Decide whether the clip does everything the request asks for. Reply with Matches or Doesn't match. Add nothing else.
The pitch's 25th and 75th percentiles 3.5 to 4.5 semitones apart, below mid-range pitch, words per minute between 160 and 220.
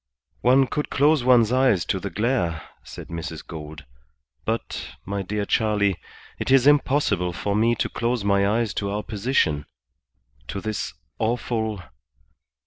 Doesn't match